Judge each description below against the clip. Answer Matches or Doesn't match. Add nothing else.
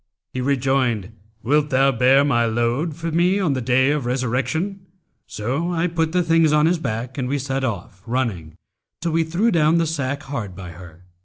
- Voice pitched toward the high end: Doesn't match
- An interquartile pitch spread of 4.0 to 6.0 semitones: Matches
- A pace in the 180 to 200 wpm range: Matches